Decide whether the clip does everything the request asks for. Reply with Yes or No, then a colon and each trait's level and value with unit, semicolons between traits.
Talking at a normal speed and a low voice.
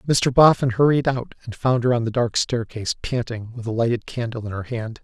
No: fast, 225 wpm; low, 120 Hz